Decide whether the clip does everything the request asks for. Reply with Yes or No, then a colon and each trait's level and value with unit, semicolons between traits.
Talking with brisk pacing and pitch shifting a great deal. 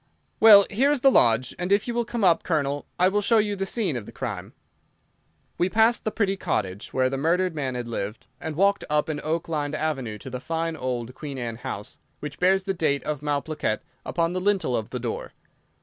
Yes: fast, 220 wpm; wide, 6.9 semitones